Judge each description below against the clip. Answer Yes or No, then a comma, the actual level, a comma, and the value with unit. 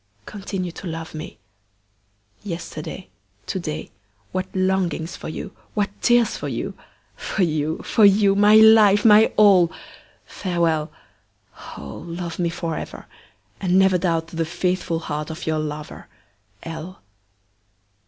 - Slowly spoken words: Yes, slow, 125 wpm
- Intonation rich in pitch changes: No, average, 3.3 semitones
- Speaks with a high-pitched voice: No, medium, 175 Hz